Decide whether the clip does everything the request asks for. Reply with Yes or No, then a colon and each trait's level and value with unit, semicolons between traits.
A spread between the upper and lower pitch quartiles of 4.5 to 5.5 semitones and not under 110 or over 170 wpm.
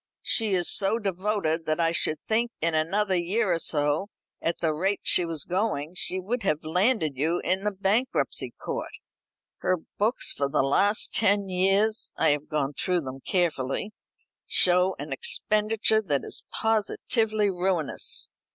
Yes: average, 4.9 semitones; average, 155 wpm